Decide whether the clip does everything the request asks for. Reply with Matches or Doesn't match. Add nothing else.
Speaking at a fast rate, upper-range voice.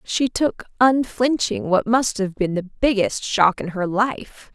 Doesn't match